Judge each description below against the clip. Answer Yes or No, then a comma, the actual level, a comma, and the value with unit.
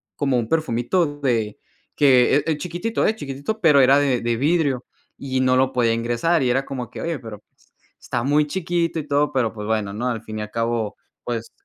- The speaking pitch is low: Yes, low, 130 Hz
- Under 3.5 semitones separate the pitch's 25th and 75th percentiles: No, average, 4.3 semitones